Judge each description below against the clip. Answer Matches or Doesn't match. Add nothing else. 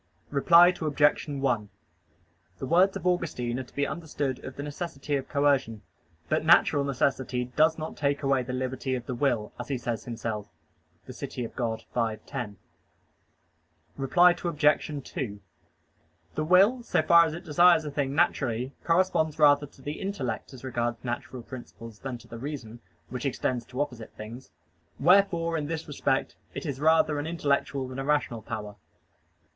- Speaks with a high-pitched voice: Doesn't match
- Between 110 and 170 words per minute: Matches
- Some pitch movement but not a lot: Matches